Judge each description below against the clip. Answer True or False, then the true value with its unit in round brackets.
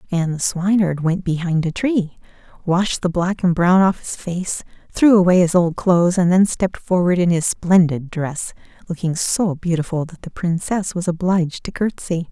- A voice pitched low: False (175 Hz)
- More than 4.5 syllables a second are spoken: True (4.9 syllables/s)